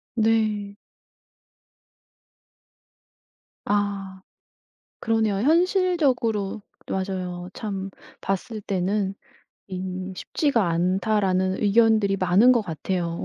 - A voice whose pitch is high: Yes, high, 200 Hz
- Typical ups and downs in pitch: Yes, average, 3.0 semitones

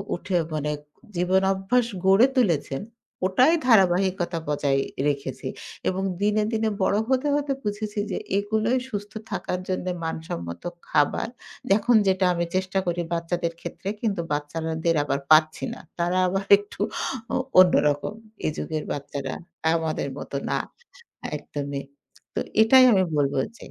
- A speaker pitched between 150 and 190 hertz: Yes, medium, 185 Hz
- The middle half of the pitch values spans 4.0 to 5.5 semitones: Yes, average, 4.9 semitones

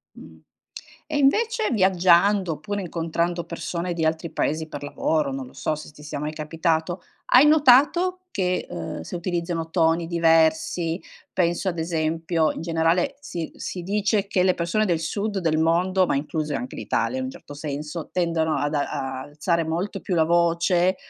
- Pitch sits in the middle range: Yes, medium, 170 Hz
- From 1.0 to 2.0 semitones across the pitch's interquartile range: No, average, 2.8 semitones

